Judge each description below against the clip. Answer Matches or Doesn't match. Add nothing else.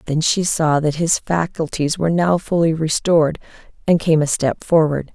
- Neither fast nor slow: Matches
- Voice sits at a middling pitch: Matches